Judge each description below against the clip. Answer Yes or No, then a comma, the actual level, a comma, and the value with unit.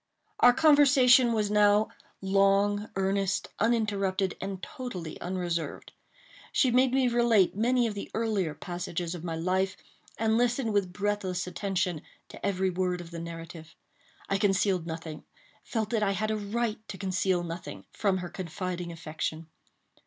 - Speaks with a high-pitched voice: Yes, high, 195 Hz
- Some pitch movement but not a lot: Yes, average, 3.6 semitones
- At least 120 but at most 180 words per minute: Yes, average, 140 wpm